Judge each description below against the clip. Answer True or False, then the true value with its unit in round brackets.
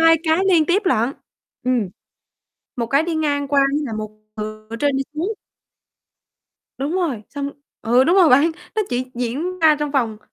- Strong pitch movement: False (4.9 semitones)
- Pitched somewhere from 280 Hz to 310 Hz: True (285 Hz)